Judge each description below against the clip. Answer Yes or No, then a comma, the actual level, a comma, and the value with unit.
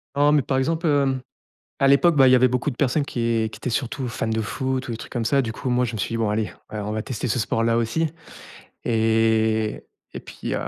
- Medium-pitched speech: No, low, 120 Hz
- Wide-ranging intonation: No, average, 3.3 semitones